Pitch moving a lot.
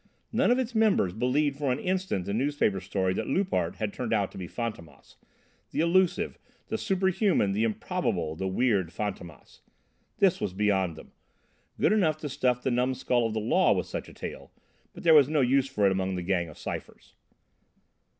Yes: wide, 8.0 semitones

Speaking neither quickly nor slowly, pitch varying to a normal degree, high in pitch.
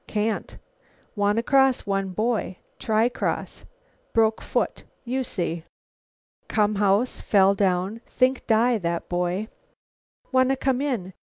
No: slow, 120 wpm; average, 4.1 semitones; high, 215 Hz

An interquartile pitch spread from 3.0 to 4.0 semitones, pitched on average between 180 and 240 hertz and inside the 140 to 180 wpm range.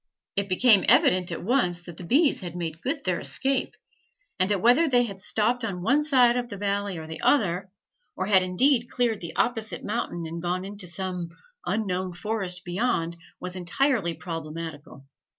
No: average, 5.3 semitones; high, 190 Hz; average, 175 wpm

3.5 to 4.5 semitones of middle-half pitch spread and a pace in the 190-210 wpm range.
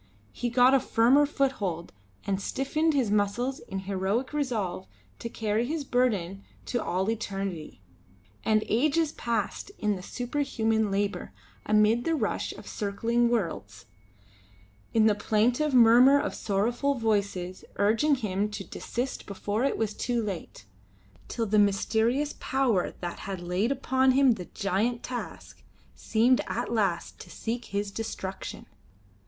No: average, 4.0 semitones; slow, 135 wpm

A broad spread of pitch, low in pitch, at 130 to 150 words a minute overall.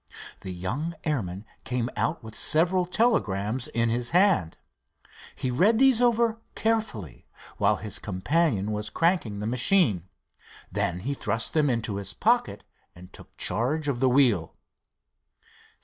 Yes: wide, 8.7 semitones; low, 125 Hz; slow, 135 wpm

